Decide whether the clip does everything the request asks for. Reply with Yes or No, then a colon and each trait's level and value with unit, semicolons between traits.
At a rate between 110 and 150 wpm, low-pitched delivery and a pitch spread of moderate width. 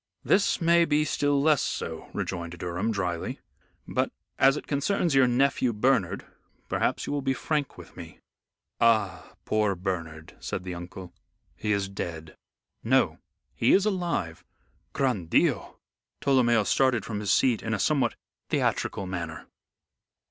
No: average, 140 wpm; low, 115 Hz; wide, 7.2 semitones